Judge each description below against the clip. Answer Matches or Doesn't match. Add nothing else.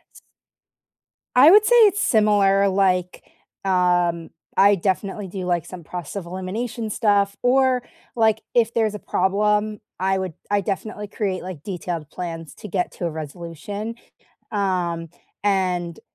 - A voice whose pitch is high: Matches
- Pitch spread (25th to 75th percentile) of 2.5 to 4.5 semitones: Matches